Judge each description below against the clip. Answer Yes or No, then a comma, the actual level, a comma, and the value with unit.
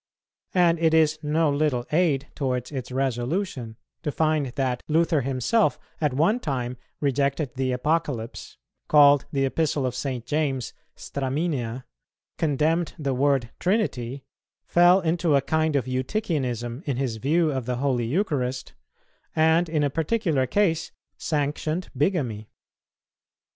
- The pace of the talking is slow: Yes, slow, 130 wpm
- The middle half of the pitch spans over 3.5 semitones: Yes, average, 3.9 semitones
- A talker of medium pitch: Yes, medium, 145 Hz